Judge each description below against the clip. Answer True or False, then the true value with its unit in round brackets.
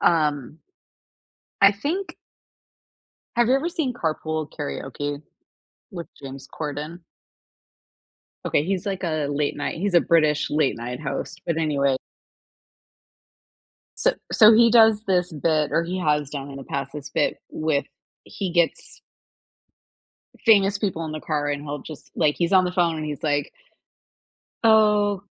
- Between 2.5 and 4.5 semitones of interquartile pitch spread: False (5.1 semitones)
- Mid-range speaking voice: True (160 Hz)